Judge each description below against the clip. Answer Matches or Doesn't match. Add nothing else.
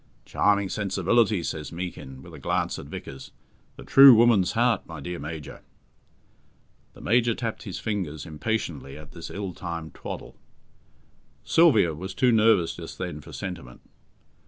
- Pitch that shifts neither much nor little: Doesn't match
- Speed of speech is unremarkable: Matches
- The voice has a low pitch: Matches